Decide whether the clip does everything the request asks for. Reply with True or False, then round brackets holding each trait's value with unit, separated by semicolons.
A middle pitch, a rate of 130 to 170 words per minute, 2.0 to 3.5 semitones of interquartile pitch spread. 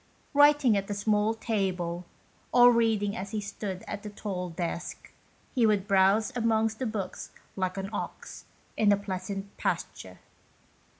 False (205 Hz; 145 wpm; 2.6 semitones)